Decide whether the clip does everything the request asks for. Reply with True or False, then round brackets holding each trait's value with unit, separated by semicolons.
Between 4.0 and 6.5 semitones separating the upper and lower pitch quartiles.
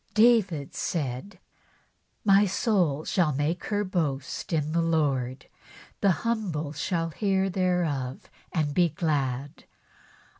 True (4.9 semitones)